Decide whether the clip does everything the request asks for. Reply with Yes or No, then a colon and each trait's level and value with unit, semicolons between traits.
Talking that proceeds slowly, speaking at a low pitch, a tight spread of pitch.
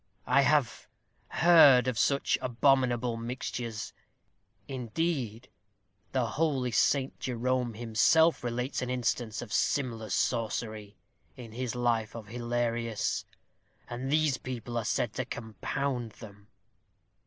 Yes: slow, 110 wpm; low, 120 Hz; narrow, 2.3 semitones